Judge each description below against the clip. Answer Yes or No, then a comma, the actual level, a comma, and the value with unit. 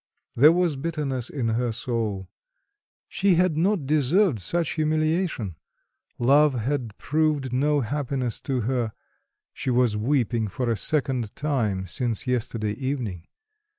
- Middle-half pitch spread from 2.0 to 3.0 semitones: No, average, 4.7 semitones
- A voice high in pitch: No, low, 130 Hz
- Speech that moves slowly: Yes, slow, 125 wpm